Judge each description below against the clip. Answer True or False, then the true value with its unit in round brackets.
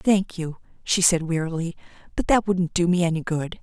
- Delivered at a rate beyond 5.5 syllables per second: False (5.1 syllables/s)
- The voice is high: False (170 Hz)